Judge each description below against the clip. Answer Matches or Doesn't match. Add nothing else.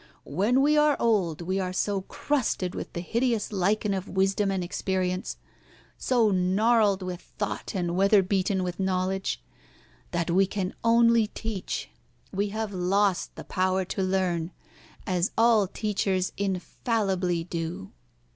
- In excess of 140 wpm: Doesn't match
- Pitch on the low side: Doesn't match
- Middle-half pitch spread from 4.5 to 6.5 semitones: Doesn't match